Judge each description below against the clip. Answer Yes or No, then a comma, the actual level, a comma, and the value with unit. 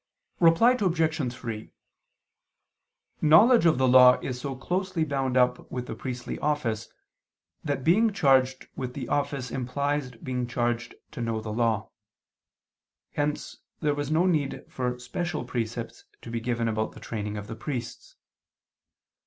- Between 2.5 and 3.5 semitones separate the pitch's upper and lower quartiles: No, average, 4.1 semitones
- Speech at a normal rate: Yes, average, 145 wpm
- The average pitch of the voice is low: Yes, low, 130 Hz